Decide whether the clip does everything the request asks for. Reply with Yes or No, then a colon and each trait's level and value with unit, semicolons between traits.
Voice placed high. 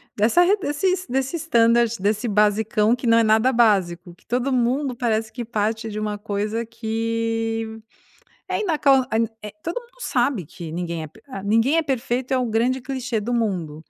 Yes: high, 230 Hz